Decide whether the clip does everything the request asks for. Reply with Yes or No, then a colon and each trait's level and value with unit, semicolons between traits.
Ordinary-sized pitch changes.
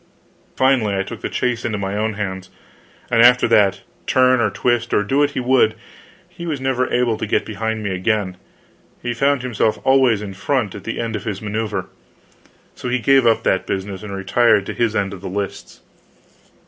Yes: average, 3.7 semitones